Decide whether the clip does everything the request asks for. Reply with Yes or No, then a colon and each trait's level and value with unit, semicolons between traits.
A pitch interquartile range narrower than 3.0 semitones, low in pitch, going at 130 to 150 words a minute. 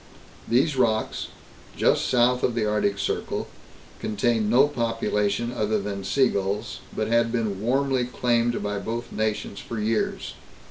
Yes: narrow, 2.6 semitones; low, 115 Hz; average, 140 wpm